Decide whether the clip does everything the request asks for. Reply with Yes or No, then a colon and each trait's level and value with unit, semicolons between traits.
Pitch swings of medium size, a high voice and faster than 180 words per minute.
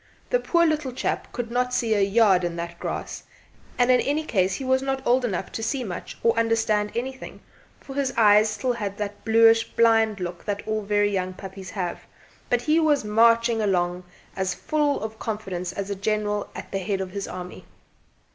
Yes: average, 3.9 semitones; high, 215 Hz; average, 195 wpm